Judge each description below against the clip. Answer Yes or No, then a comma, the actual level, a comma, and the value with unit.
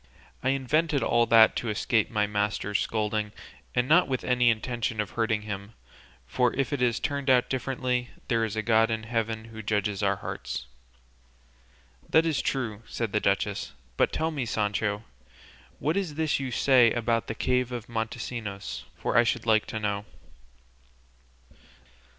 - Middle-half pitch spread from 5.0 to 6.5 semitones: No, average, 3.0 semitones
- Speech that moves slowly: No, average, 160 wpm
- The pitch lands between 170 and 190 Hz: No, low, 115 Hz